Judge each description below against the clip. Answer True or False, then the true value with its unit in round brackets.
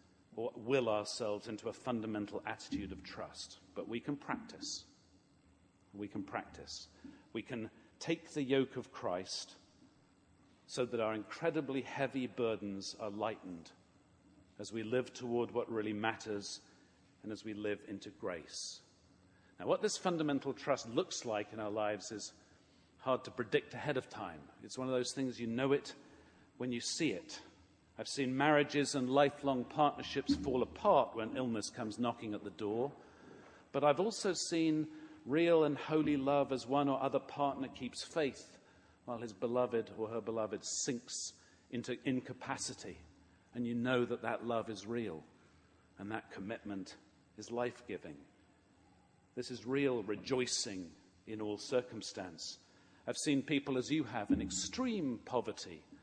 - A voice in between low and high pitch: False (120 Hz)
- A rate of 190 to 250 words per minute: False (150 wpm)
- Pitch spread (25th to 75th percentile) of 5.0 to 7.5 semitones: False (4.6 semitones)